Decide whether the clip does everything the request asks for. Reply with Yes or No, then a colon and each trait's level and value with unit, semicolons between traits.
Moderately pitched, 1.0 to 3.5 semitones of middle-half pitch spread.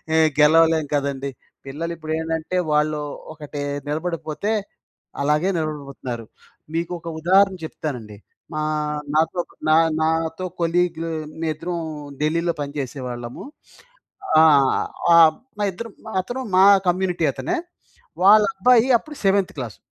Yes: medium, 160 Hz; average, 3.1 semitones